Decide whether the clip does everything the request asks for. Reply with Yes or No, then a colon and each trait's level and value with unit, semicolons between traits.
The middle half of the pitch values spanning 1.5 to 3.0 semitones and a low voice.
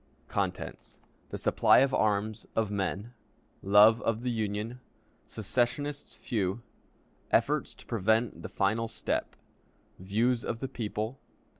Yes: narrow, 2.6 semitones; low, 110 Hz